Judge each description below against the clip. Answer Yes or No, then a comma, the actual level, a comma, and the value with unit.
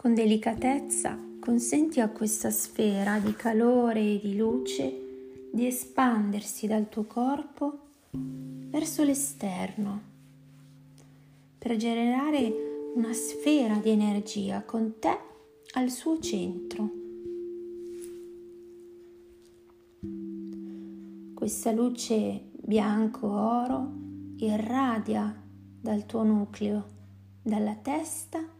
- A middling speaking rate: No, slow, 80 wpm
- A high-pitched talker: Yes, high, 215 Hz